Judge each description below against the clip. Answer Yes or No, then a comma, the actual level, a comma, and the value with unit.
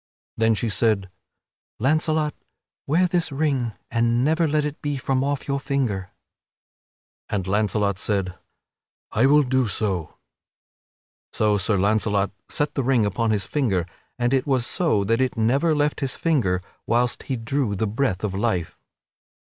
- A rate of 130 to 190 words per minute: Yes, average, 150 wpm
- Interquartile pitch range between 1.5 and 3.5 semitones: No, wide, 5.4 semitones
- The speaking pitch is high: No, low, 120 Hz